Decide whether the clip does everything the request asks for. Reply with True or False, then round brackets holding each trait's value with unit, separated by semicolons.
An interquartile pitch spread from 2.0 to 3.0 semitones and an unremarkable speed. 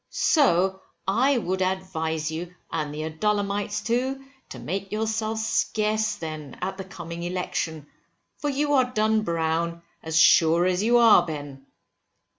False (5.0 semitones; 145 wpm)